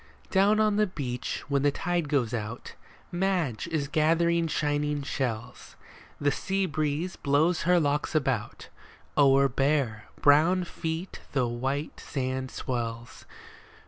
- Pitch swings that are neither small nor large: Yes, average, 4.3 semitones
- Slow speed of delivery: Yes, slow, 125 wpm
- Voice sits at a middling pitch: Yes, medium, 145 Hz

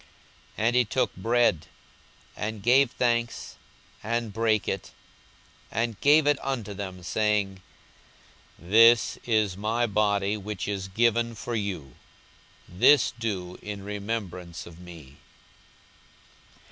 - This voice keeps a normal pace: No, slow, 110 wpm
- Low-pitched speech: Yes, low, 105 Hz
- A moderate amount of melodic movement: Yes, average, 3.5 semitones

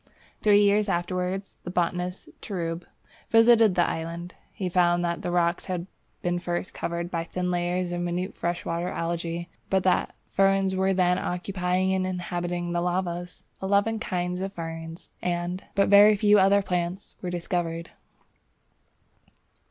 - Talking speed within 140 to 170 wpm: Yes, average, 145 wpm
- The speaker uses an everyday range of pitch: No, narrow, 1.7 semitones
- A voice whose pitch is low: No, medium, 180 Hz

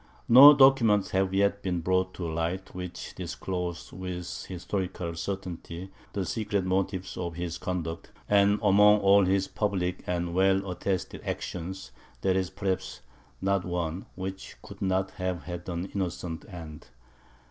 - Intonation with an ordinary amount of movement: No, narrow, 1.9 semitones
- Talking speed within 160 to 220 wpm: No, average, 140 wpm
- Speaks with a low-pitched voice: Yes, very low, 95 Hz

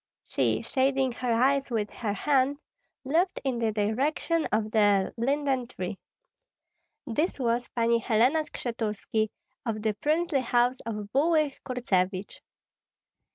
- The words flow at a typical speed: No, slow, 120 wpm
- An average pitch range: Yes, average, 4.2 semitones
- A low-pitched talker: No, high, 245 Hz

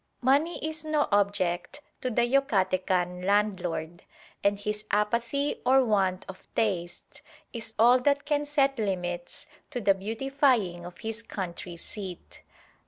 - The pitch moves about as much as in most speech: No, wide, 6.0 semitones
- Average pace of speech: No, slow, 130 wpm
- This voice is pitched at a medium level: No, high, 210 Hz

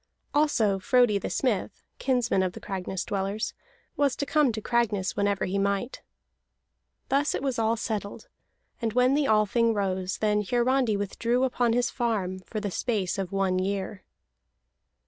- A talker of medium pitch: No, high, 215 Hz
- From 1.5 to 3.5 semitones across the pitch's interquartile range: No, average, 3.9 semitones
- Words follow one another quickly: No, average, 155 wpm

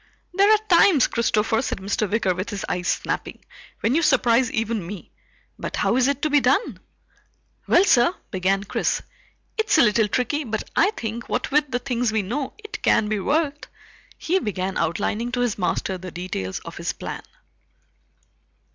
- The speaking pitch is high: Yes, high, 235 Hz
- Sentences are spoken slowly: No, average, 175 wpm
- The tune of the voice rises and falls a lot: Yes, wide, 5.9 semitones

